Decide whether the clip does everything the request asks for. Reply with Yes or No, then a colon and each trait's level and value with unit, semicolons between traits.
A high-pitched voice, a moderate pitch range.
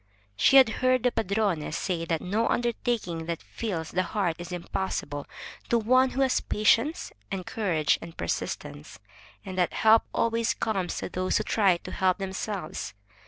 Yes: high, 195 Hz; average, 4.9 semitones